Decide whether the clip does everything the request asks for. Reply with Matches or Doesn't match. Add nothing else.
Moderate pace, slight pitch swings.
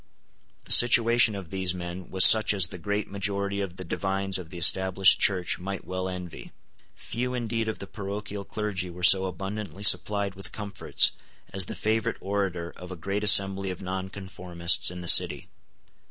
Matches